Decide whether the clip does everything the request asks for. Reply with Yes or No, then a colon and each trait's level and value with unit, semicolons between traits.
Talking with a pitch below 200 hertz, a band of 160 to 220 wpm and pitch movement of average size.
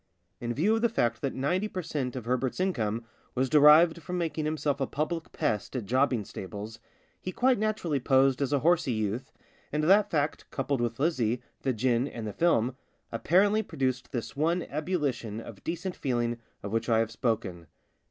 No: low, 135 Hz; average, 180 wpm; wide, 5.9 semitones